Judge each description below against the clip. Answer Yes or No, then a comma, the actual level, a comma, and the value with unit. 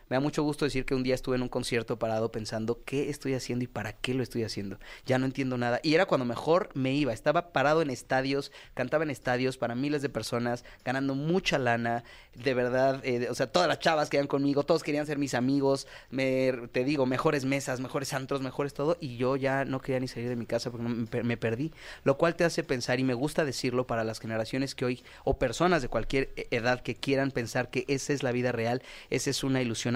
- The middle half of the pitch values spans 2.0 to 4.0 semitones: Yes, narrow, 2.5 semitones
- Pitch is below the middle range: Yes, low, 130 Hz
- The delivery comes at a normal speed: No, fast, 230 wpm